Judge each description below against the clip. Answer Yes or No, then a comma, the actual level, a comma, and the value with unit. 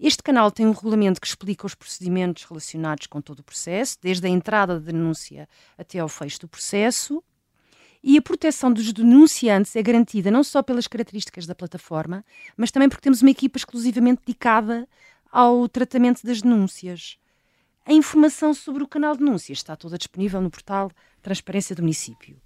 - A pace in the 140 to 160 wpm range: No, average, 175 wpm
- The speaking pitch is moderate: No, high, 210 Hz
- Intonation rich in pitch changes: Yes, wide, 6.1 semitones